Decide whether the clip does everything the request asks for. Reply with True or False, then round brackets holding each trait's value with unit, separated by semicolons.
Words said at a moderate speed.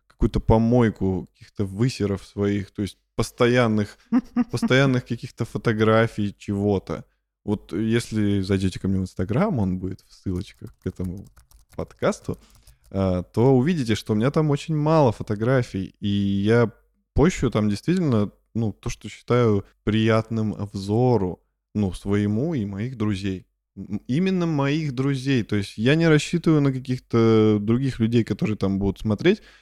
True (135 wpm)